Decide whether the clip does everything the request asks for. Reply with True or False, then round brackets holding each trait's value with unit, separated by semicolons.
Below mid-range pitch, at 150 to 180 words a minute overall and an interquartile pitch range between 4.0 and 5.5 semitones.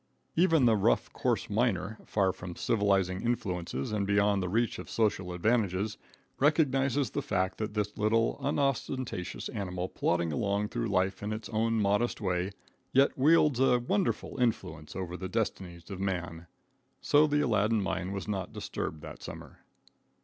True (105 Hz; 155 wpm; 4.4 semitones)